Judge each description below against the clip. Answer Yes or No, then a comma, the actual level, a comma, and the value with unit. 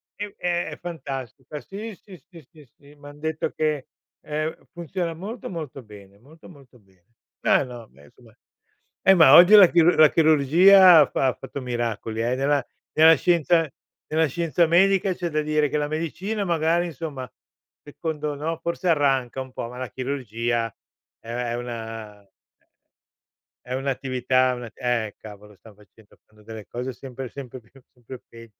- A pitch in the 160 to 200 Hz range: No, medium, 140 Hz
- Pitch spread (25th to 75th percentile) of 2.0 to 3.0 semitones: No, average, 5.2 semitones